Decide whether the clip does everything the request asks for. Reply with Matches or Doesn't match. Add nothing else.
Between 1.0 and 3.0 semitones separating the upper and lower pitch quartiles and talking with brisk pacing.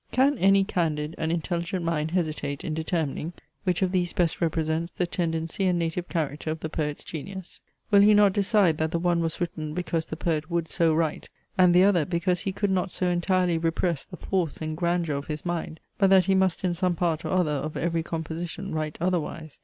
Matches